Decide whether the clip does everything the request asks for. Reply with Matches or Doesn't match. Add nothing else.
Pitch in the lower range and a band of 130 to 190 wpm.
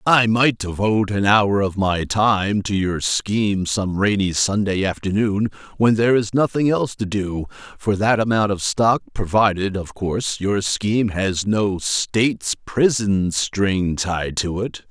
Matches